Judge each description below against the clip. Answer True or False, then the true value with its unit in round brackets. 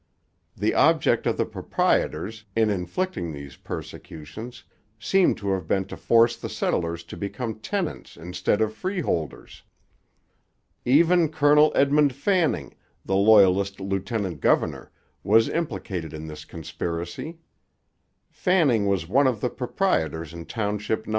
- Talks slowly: True (125 wpm)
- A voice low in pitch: True (105 Hz)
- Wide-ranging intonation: True (7.7 semitones)